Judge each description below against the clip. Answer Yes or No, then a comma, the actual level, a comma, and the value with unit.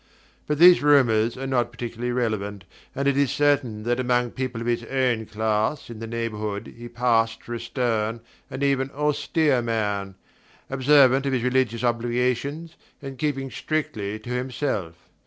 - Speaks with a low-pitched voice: Yes, low, 120 Hz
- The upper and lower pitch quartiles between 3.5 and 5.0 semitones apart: No, average, 3.0 semitones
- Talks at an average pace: Yes, average, 155 wpm